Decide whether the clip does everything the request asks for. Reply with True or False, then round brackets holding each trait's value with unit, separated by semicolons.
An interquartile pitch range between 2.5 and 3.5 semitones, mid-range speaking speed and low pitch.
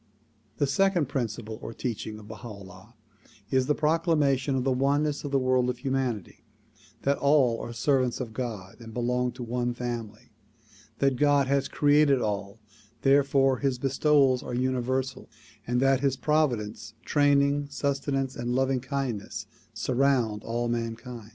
True (2.8 semitones; 150 wpm; 130 Hz)